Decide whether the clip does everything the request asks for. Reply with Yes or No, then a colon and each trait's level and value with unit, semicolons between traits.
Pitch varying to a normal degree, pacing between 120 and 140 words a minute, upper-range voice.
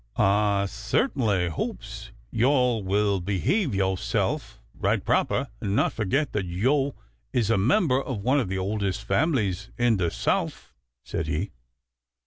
No: average, 5.0 semitones; slow, 135 wpm; low, 105 Hz